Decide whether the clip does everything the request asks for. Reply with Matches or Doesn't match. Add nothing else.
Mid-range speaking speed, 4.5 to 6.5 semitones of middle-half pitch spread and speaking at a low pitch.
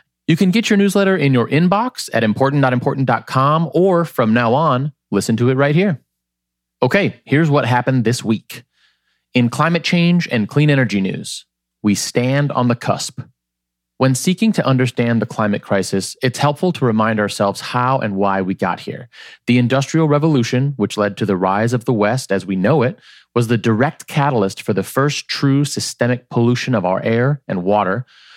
Matches